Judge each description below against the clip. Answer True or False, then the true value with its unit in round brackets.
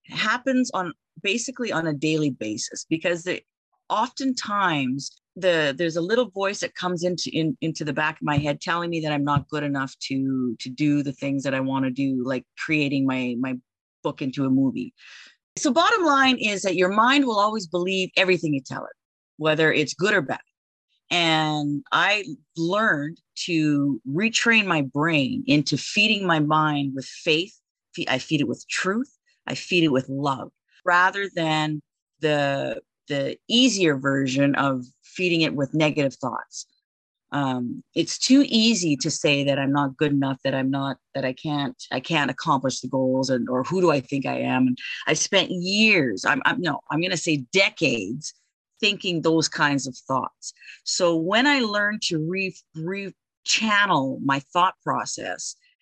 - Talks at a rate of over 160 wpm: True (170 wpm)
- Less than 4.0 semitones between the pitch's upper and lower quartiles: False (5.2 semitones)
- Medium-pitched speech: True (155 Hz)